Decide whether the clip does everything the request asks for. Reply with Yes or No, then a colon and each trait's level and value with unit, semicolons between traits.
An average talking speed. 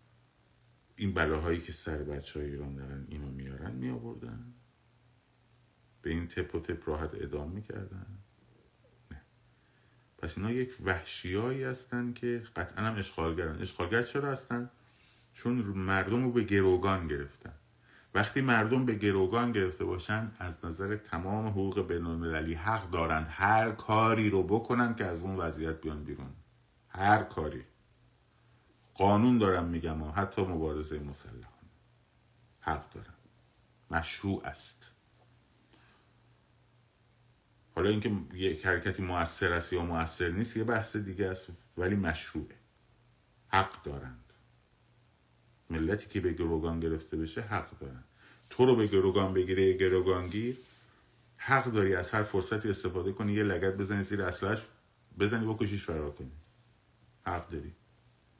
Yes: average, 130 wpm